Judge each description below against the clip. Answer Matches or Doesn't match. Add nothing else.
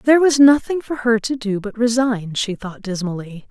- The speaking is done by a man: Doesn't match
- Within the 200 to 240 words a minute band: Matches